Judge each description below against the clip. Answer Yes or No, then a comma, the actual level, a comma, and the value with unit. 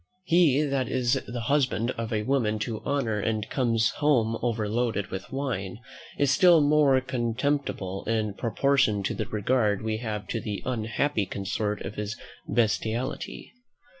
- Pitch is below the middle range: Yes, low, 115 Hz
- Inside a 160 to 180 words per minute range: No, average, 145 wpm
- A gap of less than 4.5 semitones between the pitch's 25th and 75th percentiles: Yes, average, 4.0 semitones